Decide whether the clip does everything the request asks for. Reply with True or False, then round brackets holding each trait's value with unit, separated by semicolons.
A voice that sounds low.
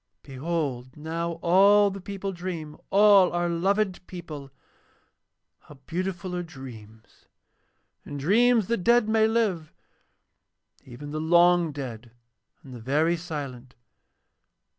False (170 Hz)